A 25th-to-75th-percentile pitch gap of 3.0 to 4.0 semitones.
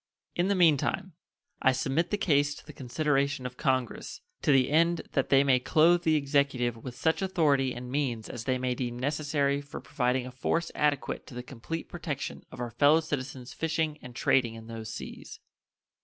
Yes: average, 3.7 semitones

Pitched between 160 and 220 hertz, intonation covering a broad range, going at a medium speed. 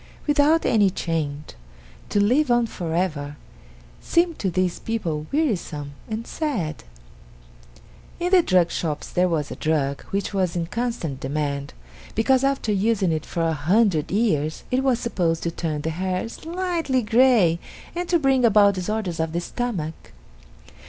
Yes: high, 190 Hz; wide, 7.1 semitones; average, 150 wpm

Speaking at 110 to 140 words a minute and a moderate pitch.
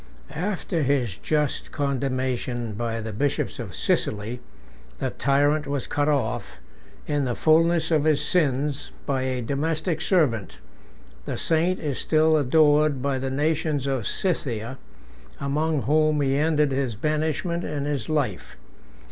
Yes: slow, 135 wpm; medium, 145 Hz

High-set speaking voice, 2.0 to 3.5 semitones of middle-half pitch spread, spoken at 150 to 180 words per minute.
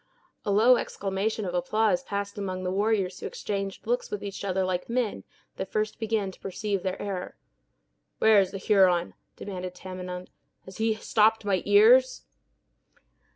Yes: high, 200 Hz; narrow, 2.6 semitones; average, 155 wpm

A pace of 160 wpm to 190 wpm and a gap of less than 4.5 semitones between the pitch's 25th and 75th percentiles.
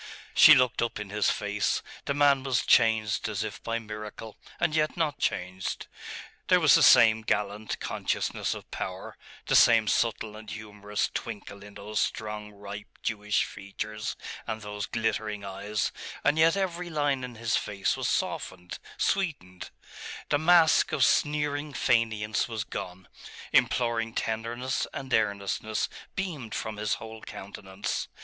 No: average, 145 wpm; average, 4.0 semitones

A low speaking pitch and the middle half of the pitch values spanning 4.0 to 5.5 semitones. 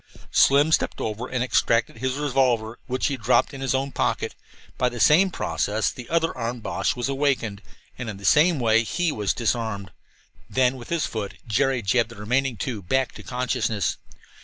No: low, 125 Hz; average, 3.3 semitones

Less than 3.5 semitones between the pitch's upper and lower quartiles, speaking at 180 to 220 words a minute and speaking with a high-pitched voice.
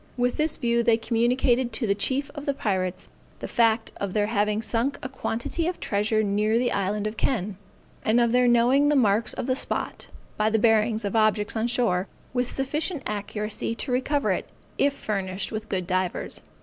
Yes: average, 3.1 semitones; average, 190 wpm; high, 225 Hz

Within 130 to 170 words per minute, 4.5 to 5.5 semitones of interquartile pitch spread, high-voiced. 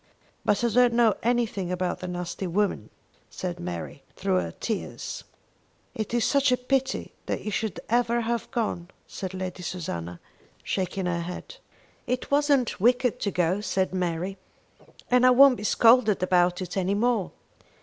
Yes: average, 160 wpm; average, 5.0 semitones; high, 200 Hz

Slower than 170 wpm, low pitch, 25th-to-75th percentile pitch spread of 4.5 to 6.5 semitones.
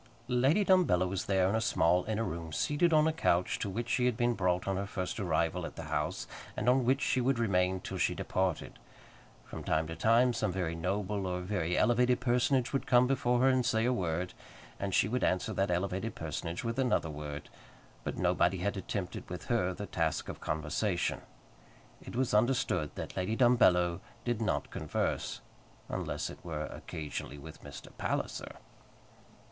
No: average, 185 wpm; low, 100 Hz; wide, 5.5 semitones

